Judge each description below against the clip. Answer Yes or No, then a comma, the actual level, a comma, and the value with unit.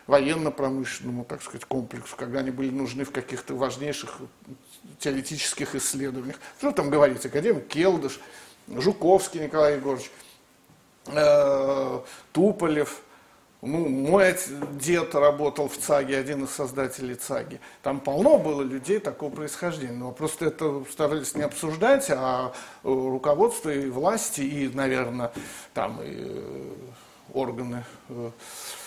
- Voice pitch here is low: No, medium, 145 Hz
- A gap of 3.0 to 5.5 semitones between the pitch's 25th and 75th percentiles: No, narrow, 2.5 semitones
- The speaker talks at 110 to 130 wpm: Yes, average, 115 wpm